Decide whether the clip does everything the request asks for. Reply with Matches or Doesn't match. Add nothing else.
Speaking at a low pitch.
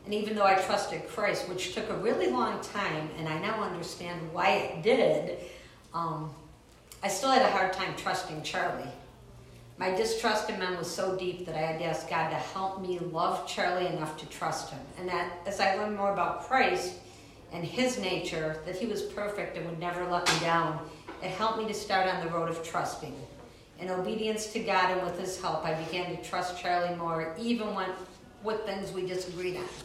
Doesn't match